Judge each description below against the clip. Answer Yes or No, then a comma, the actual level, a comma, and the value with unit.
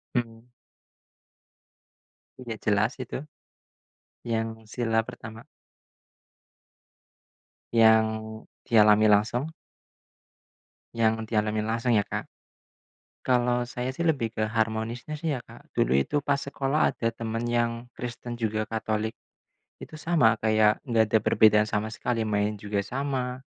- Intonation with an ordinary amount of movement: No, narrow, 2.1 semitones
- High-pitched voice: No, low, 115 Hz